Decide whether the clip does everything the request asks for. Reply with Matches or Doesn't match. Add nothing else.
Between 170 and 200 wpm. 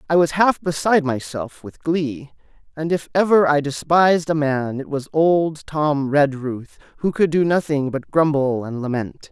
Matches